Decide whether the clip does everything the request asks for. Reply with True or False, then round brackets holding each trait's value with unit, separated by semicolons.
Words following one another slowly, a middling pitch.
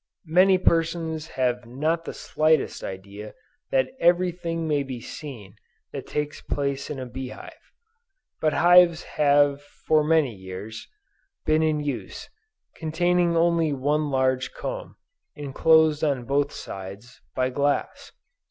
True (130 wpm; 145 Hz)